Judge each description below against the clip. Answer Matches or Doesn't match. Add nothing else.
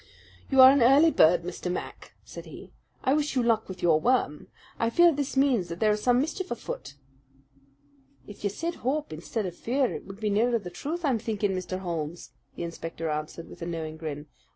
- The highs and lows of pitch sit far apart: Matches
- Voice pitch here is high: Matches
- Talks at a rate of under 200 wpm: Doesn't match